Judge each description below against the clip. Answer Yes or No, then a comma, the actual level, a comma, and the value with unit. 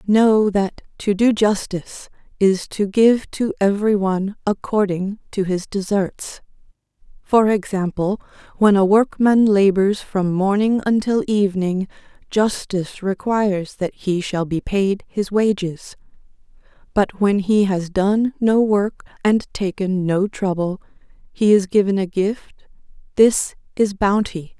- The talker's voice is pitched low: No, high, 200 Hz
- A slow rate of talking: Yes, slow, 125 wpm